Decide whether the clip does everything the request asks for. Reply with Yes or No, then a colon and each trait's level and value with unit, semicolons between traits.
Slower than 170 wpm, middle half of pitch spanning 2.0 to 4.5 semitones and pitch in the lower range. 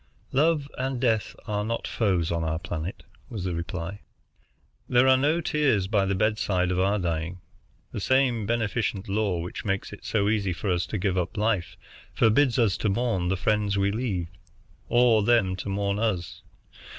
No: average, 175 wpm; average, 3.9 semitones; low, 105 Hz